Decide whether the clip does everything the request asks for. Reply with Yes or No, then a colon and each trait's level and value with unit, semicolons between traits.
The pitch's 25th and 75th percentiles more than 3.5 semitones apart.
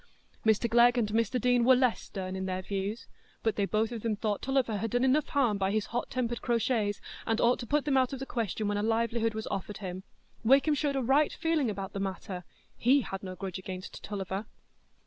Yes: average, 3.9 semitones